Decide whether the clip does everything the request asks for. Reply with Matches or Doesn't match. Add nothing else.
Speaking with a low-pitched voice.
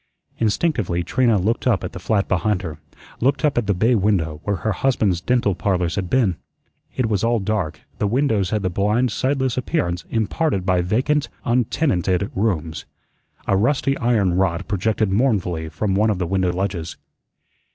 Matches